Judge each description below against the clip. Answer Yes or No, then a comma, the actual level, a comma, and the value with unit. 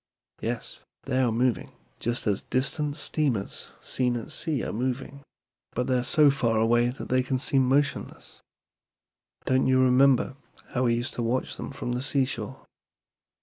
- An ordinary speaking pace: Yes, average, 155 wpm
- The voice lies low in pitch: Yes, low, 130 Hz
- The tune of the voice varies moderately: No, narrow, 2.0 semitones